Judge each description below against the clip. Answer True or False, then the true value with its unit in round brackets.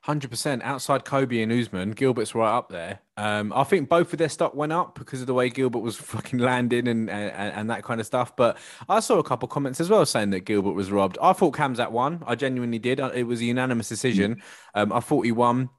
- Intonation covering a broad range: False (3.3 semitones)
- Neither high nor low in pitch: False (125 Hz)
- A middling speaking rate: False (245 wpm)